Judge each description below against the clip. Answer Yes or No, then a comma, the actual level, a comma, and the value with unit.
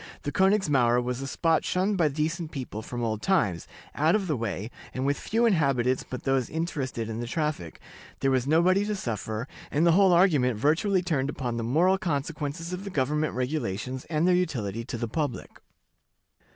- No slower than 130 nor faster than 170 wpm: No, average, 185 wpm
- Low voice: No, medium, 145 Hz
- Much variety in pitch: Yes, wide, 5.7 semitones